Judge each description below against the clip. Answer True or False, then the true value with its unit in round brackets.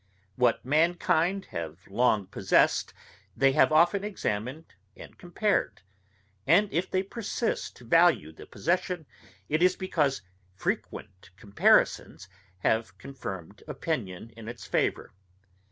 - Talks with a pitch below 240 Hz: True (140 Hz)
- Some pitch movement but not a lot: False (8.6 semitones)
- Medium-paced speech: False (115 wpm)